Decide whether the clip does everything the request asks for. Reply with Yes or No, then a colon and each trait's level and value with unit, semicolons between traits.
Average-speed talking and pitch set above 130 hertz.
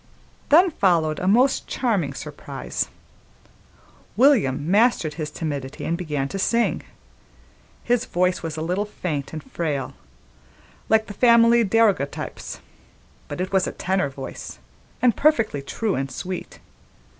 No: slow, 130 wpm; medium, 185 Hz